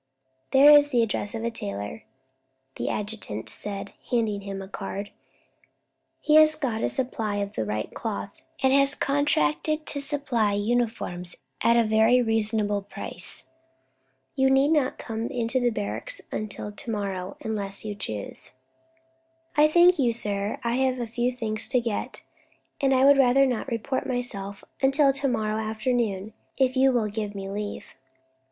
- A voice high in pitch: Yes, high, 225 Hz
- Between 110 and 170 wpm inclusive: Yes, average, 155 wpm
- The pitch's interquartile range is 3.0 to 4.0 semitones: No, average, 4.5 semitones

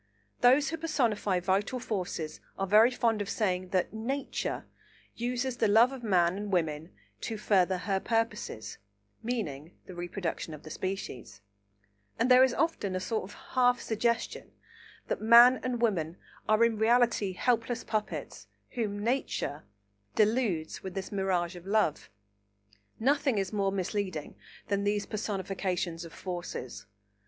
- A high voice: Yes, high, 205 Hz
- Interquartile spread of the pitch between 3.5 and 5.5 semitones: Yes, average, 4.3 semitones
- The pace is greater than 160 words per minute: No, average, 140 wpm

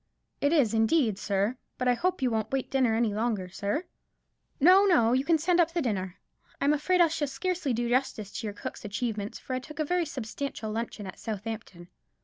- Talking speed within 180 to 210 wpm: Yes, fast, 205 wpm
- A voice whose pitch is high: Yes, high, 245 Hz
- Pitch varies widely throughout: Yes, wide, 5.9 semitones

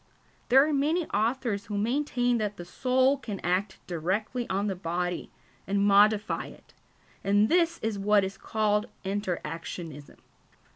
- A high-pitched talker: Yes, high, 210 Hz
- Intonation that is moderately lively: Yes, average, 4.2 semitones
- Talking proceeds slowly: No, average, 145 wpm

